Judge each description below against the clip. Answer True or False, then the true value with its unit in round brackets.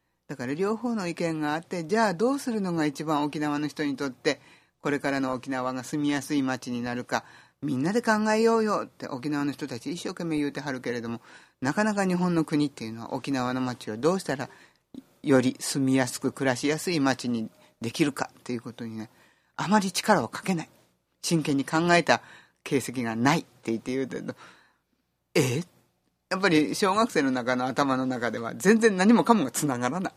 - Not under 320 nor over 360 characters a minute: False (375 characters per minute)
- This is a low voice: False (145 Hz)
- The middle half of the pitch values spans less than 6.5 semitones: True (5.2 semitones)